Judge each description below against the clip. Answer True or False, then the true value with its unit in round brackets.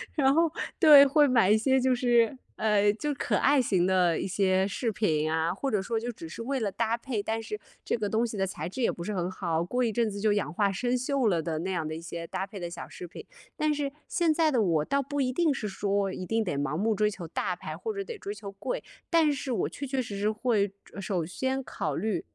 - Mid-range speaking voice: False (215 Hz)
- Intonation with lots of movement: True (5.8 semitones)